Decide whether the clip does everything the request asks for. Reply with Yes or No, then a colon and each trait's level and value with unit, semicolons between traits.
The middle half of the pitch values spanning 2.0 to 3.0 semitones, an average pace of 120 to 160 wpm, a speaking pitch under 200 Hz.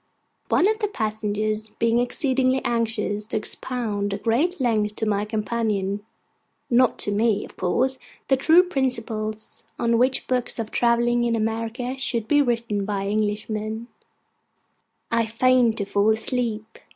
No: average, 2.7 semitones; average, 140 wpm; high, 230 Hz